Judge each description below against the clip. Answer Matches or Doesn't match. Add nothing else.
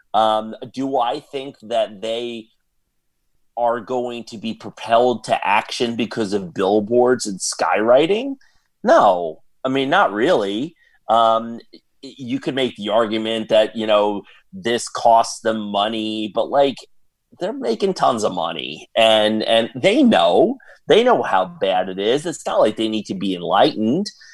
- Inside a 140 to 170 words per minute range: Matches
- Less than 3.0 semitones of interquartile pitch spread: Matches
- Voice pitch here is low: Matches